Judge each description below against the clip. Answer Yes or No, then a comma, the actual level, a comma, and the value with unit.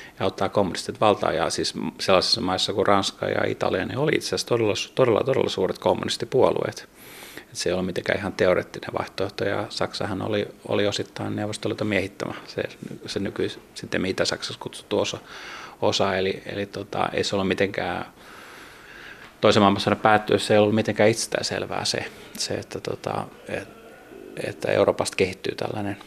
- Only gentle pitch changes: Yes, narrow, 1.3 semitones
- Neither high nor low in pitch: No, low, 105 Hz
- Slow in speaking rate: No, average, 150 wpm